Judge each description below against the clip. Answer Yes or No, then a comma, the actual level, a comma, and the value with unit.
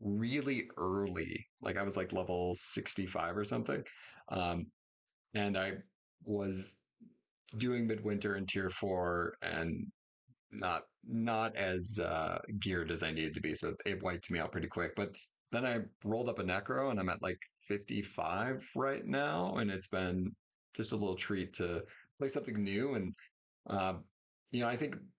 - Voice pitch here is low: Yes, very low, 95 Hz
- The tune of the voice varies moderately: Yes, average, 3.0 semitones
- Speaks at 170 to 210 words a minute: No, average, 160 wpm